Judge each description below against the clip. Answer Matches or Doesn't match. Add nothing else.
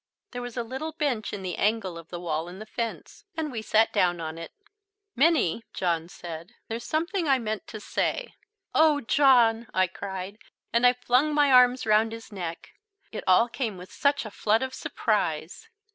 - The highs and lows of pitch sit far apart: Matches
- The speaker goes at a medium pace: Matches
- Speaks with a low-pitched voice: Doesn't match